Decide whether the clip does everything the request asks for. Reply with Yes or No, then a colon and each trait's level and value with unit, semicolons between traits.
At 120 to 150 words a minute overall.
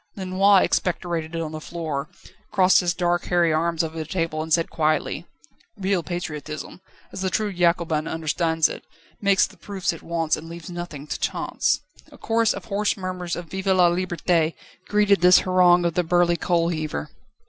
No: average, 175 wpm